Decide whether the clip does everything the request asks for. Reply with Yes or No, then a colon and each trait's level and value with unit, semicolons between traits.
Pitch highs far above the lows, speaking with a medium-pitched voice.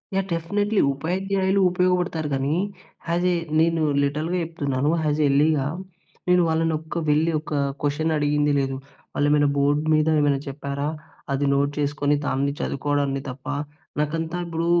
No: average, 2.8 semitones; medium, 150 Hz